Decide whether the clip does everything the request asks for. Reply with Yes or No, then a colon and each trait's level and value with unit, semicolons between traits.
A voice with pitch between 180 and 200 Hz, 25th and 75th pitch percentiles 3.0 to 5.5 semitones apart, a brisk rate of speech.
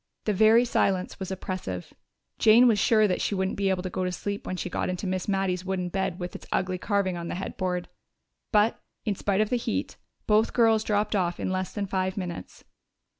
No: high, 190 Hz; narrow, 2.4 semitones; fast, 215 wpm